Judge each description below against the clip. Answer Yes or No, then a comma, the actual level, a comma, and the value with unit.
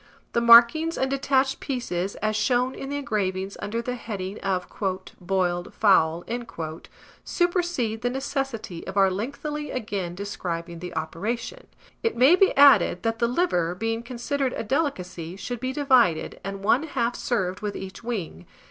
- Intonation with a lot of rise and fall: Yes, wide, 5.9 semitones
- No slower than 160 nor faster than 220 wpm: No, average, 150 wpm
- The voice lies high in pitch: Yes, high, 225 Hz